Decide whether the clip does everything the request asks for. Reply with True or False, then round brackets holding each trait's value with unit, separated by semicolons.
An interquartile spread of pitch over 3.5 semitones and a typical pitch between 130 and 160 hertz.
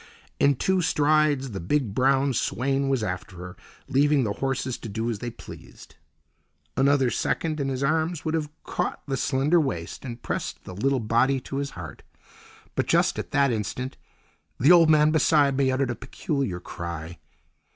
True (3.9 semitones; 135 Hz)